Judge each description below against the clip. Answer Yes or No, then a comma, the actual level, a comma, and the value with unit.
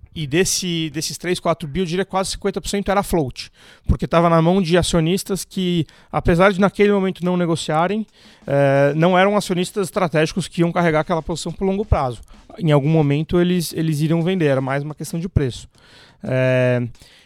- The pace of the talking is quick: No, average, 175 wpm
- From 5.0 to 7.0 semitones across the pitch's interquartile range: No, average, 3.4 semitones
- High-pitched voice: No, medium, 170 Hz